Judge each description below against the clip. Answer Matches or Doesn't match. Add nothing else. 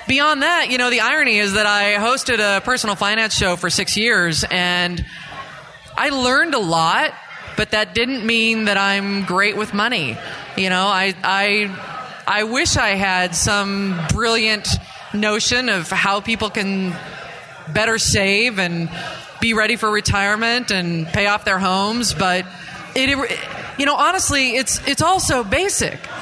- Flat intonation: Doesn't match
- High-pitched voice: Matches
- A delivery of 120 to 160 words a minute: Matches